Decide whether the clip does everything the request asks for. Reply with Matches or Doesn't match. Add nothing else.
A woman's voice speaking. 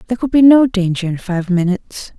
Matches